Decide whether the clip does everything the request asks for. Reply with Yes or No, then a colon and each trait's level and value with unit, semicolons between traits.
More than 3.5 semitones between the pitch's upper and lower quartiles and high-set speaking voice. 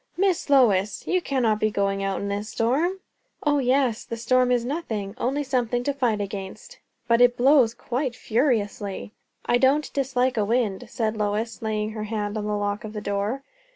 Yes: average, 3.9 semitones; high, 230 Hz